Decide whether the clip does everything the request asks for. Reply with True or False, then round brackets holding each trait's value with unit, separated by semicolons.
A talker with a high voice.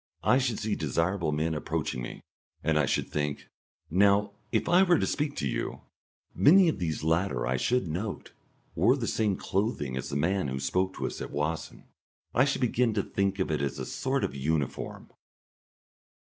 False (90 Hz)